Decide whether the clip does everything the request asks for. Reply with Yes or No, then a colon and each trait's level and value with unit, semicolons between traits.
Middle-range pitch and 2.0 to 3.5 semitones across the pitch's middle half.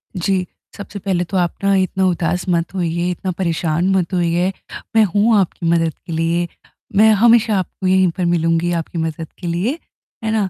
Yes: medium, 180 Hz; narrow, 2.4 semitones